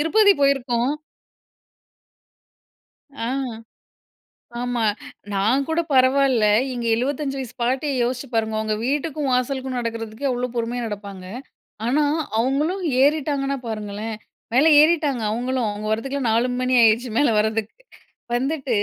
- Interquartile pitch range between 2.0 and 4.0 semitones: Yes, average, 3.5 semitones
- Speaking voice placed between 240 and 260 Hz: Yes, very high, 250 Hz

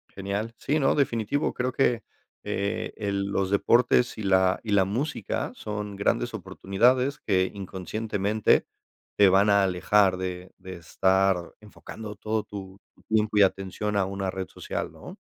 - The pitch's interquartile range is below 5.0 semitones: Yes, narrow, 2.4 semitones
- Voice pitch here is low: Yes, low, 100 Hz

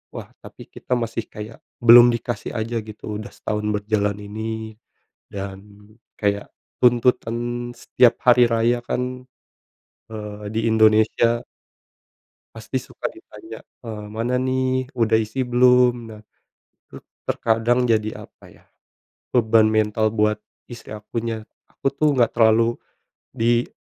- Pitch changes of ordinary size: No, narrow, 2.2 semitones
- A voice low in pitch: Yes, low, 115 Hz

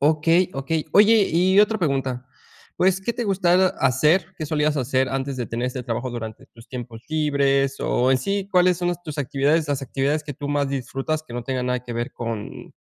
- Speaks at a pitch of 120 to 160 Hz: Yes, medium, 140 Hz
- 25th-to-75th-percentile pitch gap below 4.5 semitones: No, average, 4.8 semitones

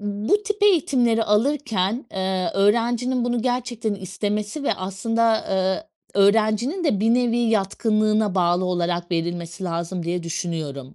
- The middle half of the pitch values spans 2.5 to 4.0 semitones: No, average, 4.5 semitones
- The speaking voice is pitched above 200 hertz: Yes, high, 210 Hz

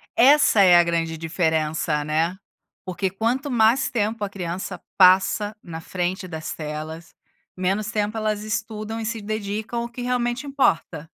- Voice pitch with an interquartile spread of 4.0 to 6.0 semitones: Yes, average, 4.8 semitones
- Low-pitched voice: No, high, 200 Hz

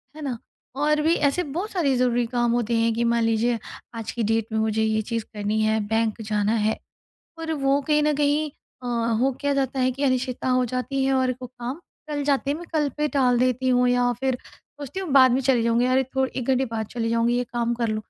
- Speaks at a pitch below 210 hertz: No, very high, 250 Hz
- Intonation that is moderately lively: Yes, average, 3.2 semitones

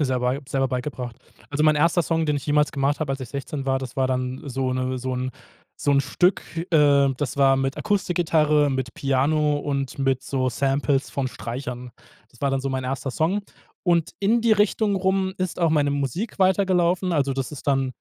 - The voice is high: No, medium, 140 Hz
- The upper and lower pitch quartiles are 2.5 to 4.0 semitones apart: Yes, average, 3.6 semitones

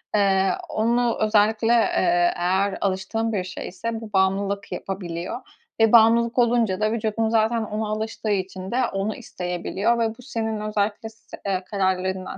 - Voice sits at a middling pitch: No, high, 210 Hz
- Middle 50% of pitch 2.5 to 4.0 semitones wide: Yes, average, 2.9 semitones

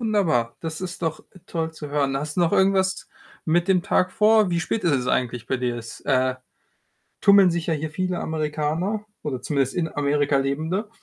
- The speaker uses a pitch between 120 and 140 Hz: No, medium, 160 Hz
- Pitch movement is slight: No, average, 4.7 semitones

